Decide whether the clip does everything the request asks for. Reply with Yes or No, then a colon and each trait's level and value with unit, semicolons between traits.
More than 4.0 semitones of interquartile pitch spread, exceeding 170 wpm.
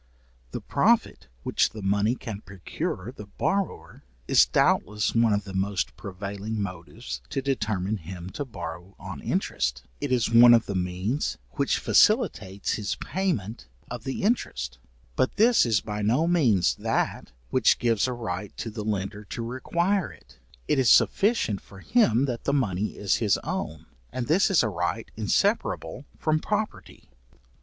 No: average, 5.3 semitones; average, 155 wpm